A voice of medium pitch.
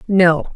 Yes: medium, 180 Hz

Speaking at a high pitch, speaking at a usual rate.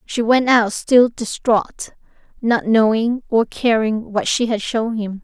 Yes: high, 225 Hz; average, 160 wpm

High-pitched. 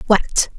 Yes: high, 205 Hz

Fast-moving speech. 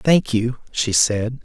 No: average, 165 wpm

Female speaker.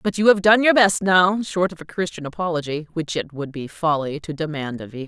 Yes: female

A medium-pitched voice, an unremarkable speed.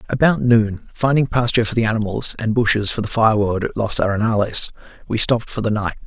No: low, 110 Hz; average, 190 wpm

